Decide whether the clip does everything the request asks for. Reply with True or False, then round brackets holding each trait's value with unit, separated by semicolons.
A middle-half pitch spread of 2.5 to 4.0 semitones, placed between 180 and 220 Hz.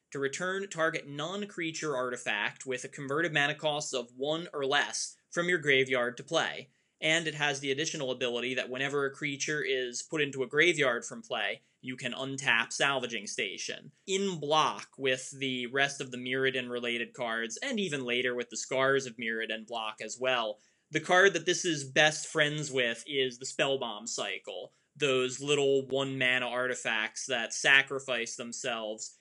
False (3.4 semitones; 135 Hz)